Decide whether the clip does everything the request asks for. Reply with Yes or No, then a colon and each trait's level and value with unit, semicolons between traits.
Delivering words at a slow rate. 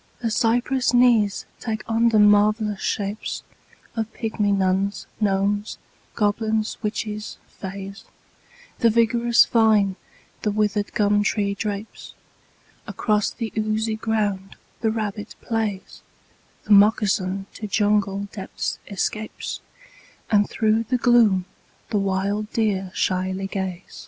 Yes: slow, 110 wpm